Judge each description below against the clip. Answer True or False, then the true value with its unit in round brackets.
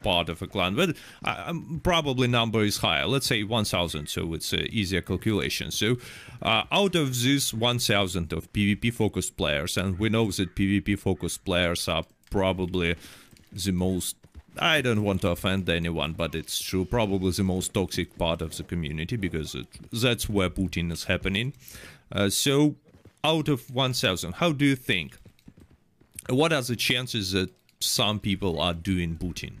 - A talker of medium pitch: False (100 Hz)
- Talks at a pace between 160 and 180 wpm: True (170 wpm)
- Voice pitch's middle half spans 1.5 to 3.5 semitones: False (5.5 semitones)